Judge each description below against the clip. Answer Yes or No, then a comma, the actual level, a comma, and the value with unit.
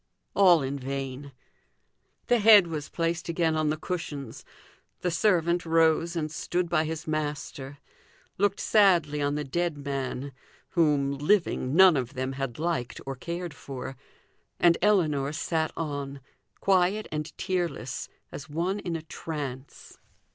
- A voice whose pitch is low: No, medium, 155 Hz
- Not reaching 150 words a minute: Yes, average, 140 wpm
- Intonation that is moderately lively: Yes, average, 3.7 semitones